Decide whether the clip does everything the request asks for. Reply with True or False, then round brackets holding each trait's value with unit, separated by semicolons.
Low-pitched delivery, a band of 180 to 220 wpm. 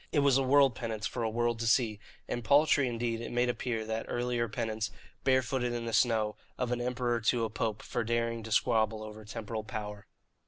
True (115 Hz; 205 wpm)